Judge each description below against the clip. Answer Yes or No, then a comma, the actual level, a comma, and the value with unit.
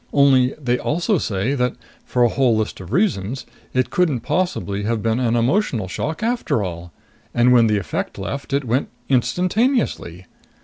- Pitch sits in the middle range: No, low, 125 Hz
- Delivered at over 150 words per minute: Yes, average, 165 wpm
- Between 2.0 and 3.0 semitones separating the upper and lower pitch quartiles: No, average, 5.3 semitones